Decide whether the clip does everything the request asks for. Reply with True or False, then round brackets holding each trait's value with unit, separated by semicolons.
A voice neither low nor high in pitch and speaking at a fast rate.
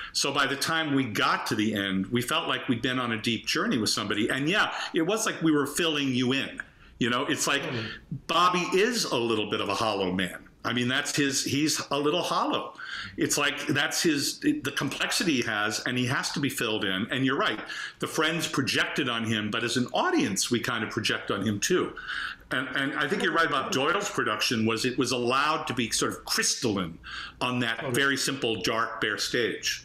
False (130 Hz; 220 wpm)